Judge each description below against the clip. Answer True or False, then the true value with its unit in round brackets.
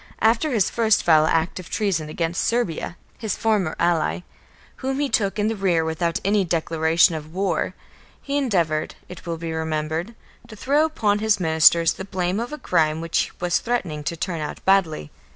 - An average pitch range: True (4.9 semitones)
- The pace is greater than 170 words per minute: True (180 wpm)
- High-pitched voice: False (180 Hz)